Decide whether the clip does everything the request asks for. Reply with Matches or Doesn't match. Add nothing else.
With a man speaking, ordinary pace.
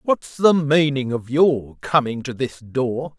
Matches